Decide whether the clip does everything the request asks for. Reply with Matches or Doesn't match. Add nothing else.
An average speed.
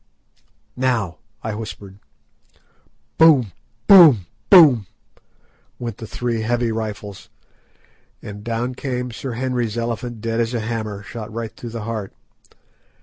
Doesn't match